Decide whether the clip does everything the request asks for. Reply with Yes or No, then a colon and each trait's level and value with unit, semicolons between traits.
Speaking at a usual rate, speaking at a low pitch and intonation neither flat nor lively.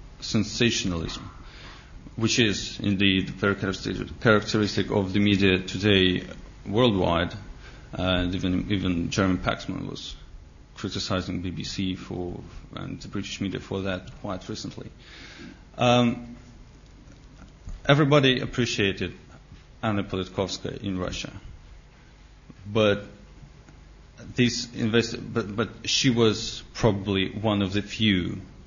No: slow, 100 wpm; low, 100 Hz; average, 3.8 semitones